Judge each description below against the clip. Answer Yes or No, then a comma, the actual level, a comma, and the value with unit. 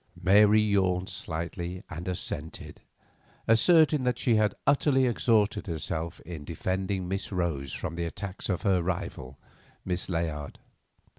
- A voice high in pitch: No, very low, 95 Hz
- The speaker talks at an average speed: No, slow, 130 wpm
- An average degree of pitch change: Yes, average, 4.0 semitones